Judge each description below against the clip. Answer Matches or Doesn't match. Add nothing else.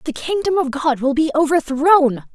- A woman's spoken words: Matches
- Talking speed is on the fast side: Doesn't match